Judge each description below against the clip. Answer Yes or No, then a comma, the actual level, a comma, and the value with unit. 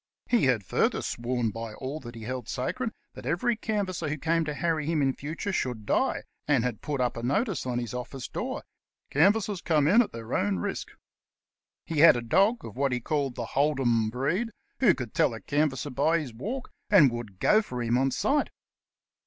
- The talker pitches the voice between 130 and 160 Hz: Yes, low, 135 Hz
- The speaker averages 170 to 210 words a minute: Yes, average, 200 wpm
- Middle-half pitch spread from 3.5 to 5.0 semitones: No, wide, 5.6 semitones